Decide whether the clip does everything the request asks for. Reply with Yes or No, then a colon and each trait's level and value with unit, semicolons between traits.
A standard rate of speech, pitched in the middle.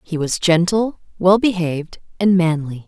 Yes: average, 145 wpm; medium, 180 Hz